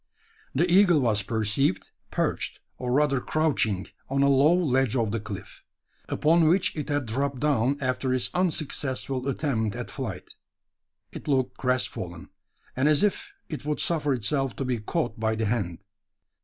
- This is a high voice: No, low, 135 Hz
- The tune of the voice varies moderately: Yes, average, 4.7 semitones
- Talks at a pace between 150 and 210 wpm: Yes, average, 155 wpm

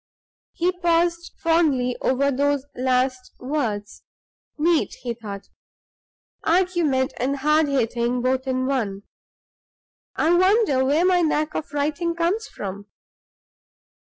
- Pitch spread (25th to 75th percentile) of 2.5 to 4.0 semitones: No, average, 4.9 semitones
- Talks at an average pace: No, slow, 110 wpm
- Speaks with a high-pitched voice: Yes, very high, 280 Hz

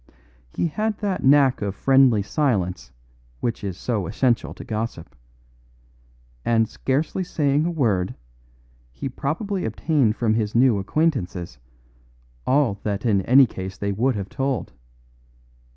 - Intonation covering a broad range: Yes, wide, 5.7 semitones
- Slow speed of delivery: Yes, slow, 130 wpm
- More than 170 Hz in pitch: No, low, 120 Hz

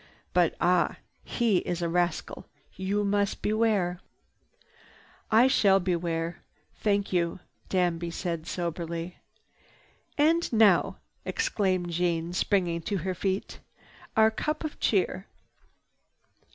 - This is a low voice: No, medium, 185 Hz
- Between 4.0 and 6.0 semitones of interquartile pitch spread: No, average, 3.3 semitones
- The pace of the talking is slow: Yes, slow, 105 wpm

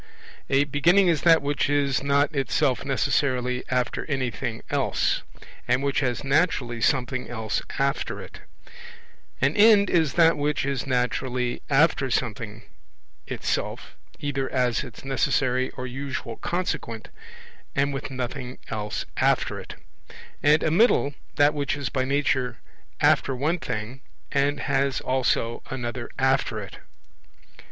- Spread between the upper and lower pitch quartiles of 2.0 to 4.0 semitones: Yes, narrow, 2.5 semitones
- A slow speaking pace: Yes, slow, 130 wpm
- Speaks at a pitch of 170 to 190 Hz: No, low, 135 Hz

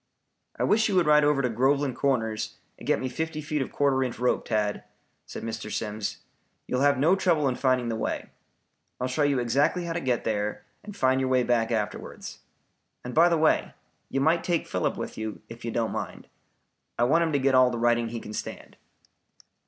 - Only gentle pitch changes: No, average, 4.4 semitones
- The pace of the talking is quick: Yes, fast, 215 wpm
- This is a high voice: No, low, 130 Hz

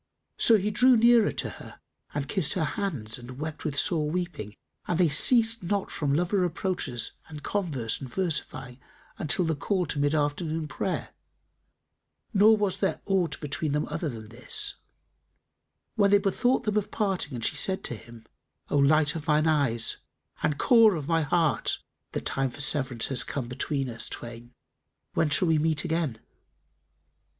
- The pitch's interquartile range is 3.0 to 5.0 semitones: No, wide, 5.5 semitones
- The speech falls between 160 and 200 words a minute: Yes, average, 170 wpm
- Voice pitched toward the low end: No, medium, 155 Hz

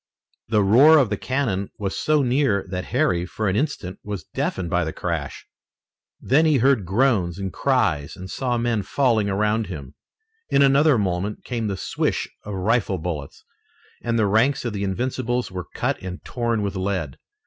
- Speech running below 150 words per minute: No, average, 175 wpm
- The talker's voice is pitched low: Yes, low, 105 Hz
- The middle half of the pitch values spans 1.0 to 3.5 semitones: No, average, 4.9 semitones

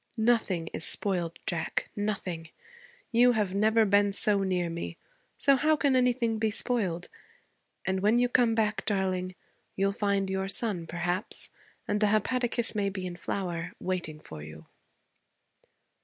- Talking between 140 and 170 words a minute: Yes, average, 145 wpm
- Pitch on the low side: No, high, 200 Hz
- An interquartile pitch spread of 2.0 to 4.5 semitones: Yes, average, 3.8 semitones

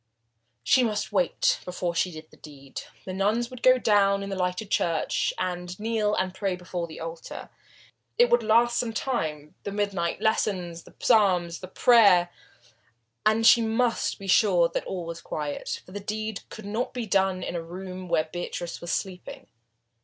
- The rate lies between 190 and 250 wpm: No, average, 175 wpm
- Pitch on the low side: No, high, 190 Hz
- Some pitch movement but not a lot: Yes, average, 3.9 semitones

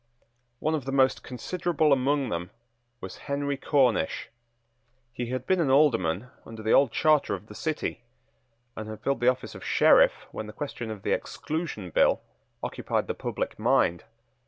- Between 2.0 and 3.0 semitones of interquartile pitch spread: No, average, 4.9 semitones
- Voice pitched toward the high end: No, low, 130 Hz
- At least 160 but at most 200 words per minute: Yes, average, 165 wpm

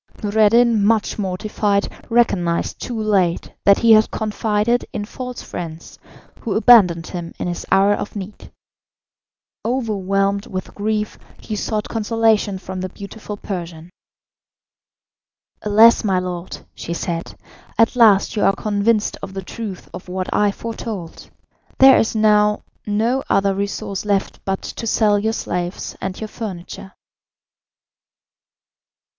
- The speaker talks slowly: Yes, slow, 130 wpm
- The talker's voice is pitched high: Yes, high, 205 Hz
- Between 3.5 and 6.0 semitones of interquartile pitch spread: No, average, 2.7 semitones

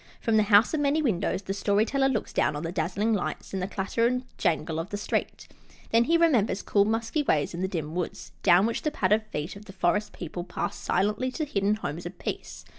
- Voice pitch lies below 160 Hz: No, high, 205 Hz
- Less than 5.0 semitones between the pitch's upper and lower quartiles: Yes, average, 4.4 semitones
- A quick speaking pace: Yes, fast, 230 wpm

